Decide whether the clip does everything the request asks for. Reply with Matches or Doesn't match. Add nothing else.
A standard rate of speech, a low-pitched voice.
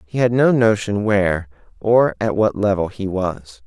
Matches